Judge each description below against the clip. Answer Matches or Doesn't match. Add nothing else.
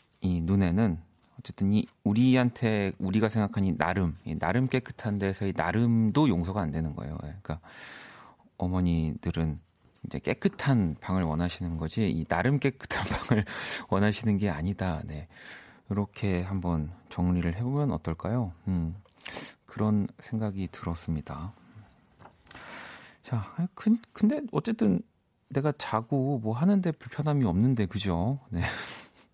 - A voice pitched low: Matches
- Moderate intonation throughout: Doesn't match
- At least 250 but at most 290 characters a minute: Matches